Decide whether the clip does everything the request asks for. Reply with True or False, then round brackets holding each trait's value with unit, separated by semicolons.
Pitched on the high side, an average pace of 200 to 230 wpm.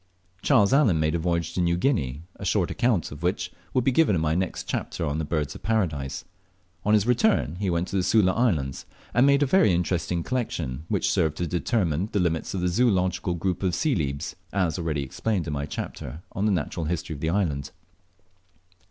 False (90 Hz; 205 wpm)